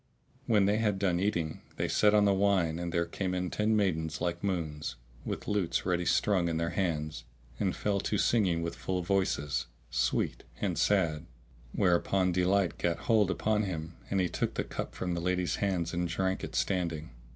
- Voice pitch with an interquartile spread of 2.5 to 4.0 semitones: Yes, average, 2.9 semitones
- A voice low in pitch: Yes, very low, 90 Hz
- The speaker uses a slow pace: No, average, 185 wpm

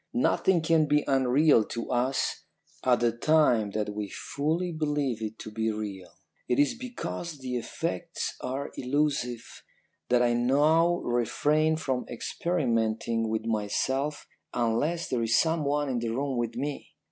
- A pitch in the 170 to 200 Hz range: No, low, 130 Hz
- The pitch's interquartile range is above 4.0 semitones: Yes, average, 4.7 semitones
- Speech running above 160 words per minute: No, average, 145 wpm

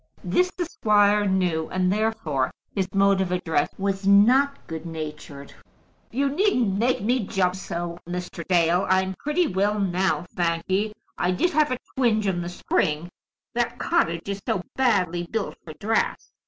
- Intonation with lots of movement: No, average, 4.2 semitones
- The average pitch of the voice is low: No, high, 190 Hz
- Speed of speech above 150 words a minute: Yes, average, 160 wpm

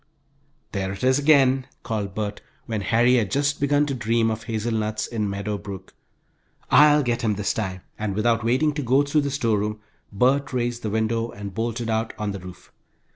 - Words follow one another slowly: No, average, 185 wpm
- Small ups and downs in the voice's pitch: No, average, 3.5 semitones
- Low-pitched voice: Yes, low, 115 Hz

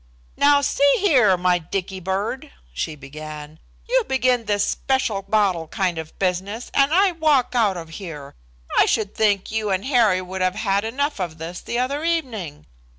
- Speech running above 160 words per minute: Yes, average, 170 wpm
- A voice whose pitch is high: Yes, high, 200 Hz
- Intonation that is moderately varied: No, wide, 6.2 semitones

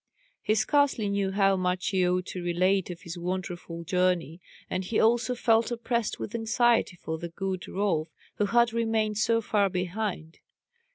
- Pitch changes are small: No, average, 3.8 semitones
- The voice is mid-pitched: No, high, 195 Hz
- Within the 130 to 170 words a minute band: Yes, average, 165 wpm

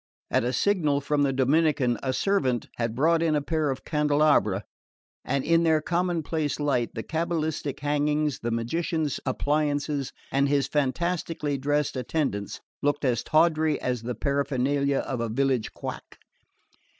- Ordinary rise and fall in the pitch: Yes, average, 3.1 semitones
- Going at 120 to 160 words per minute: Yes, average, 145 wpm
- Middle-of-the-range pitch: Yes, medium, 145 Hz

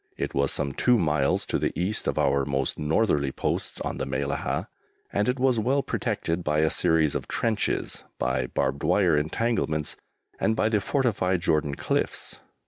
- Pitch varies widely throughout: Yes, wide, 7.5 semitones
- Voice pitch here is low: Yes, very low, 80 Hz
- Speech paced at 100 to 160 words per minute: No, average, 170 wpm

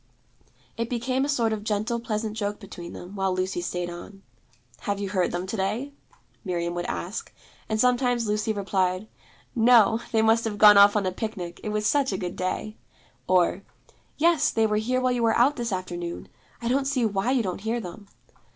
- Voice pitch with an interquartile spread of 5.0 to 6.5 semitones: No, average, 3.7 semitones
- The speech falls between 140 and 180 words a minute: No, average, 195 wpm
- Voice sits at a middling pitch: No, high, 210 Hz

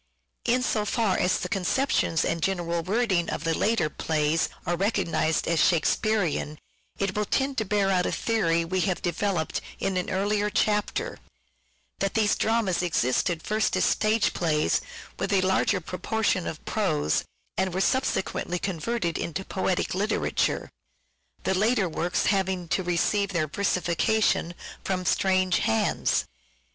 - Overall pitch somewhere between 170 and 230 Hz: Yes, medium, 185 Hz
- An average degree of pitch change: Yes, average, 3.6 semitones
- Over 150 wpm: No, average, 145 wpm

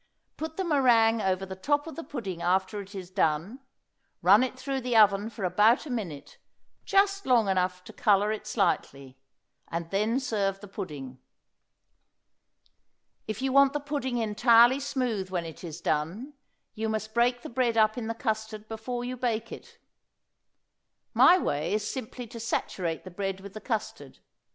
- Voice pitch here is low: No, high, 220 Hz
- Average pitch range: Yes, average, 4.7 semitones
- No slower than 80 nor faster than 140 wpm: No, average, 170 wpm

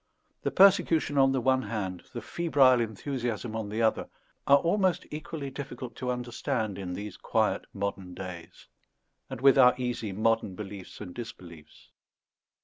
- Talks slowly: No, average, 145 wpm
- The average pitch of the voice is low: Yes, low, 120 Hz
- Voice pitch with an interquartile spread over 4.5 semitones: Yes, average, 5.0 semitones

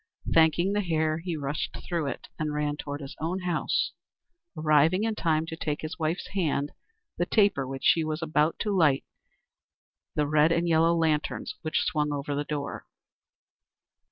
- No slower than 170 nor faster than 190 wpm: Yes, average, 175 wpm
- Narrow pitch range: Yes, narrow, 2.2 semitones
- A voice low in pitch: No, medium, 155 Hz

